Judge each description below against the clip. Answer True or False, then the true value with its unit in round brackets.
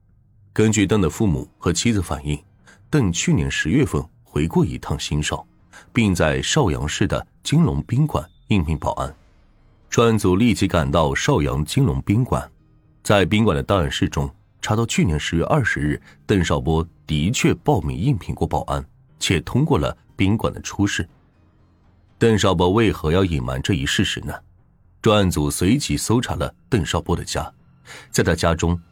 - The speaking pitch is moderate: False (90 Hz)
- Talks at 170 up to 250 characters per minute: True (245 characters per minute)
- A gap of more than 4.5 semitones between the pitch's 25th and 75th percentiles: True (5.4 semitones)